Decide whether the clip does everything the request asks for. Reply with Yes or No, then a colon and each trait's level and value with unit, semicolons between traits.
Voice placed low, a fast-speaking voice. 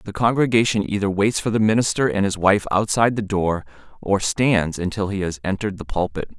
No: low, 105 Hz; average, 195 wpm